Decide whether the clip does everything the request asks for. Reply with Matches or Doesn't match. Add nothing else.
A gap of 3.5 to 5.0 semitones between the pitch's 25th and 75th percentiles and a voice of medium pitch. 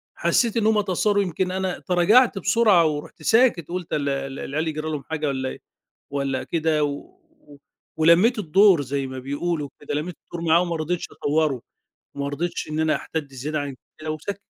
Matches